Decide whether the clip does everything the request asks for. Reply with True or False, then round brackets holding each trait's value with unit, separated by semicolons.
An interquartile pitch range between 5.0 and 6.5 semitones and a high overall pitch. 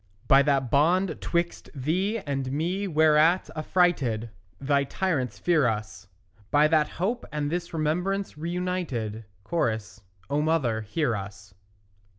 False (5.3 semitones; 150 Hz)